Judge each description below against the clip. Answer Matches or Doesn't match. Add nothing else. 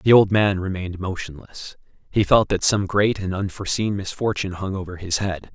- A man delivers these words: Matches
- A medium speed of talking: Matches